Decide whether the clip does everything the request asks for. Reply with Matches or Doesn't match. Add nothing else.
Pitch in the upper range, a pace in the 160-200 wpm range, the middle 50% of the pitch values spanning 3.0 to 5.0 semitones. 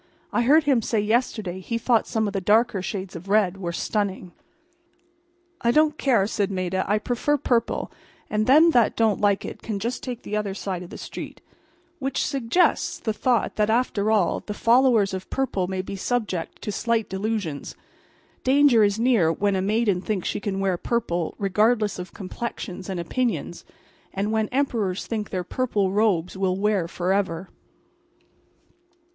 Matches